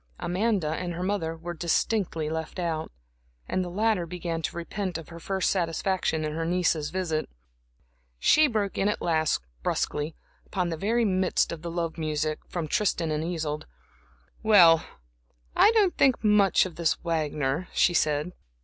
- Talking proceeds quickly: No, average, 160 wpm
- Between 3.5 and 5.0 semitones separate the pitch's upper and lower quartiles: No, average, 3.1 semitones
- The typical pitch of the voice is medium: Yes, medium, 170 Hz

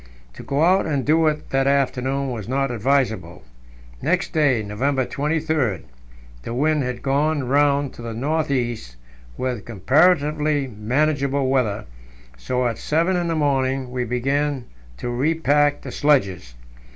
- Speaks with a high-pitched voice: No, low, 135 Hz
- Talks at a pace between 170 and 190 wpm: No, average, 140 wpm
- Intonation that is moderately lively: Yes, average, 3.5 semitones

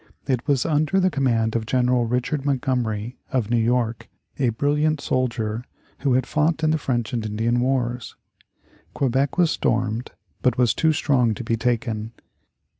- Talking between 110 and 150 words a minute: No, average, 160 wpm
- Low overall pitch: Yes, low, 125 Hz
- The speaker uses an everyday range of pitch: Yes, average, 3.3 semitones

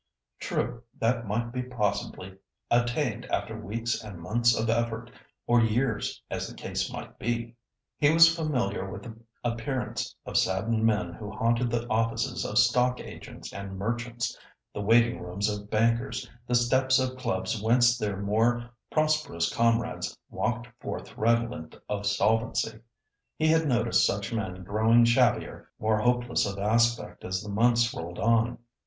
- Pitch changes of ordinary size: No, narrow, 2.2 semitones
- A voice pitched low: Yes, low, 115 Hz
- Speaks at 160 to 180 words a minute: No, average, 150 wpm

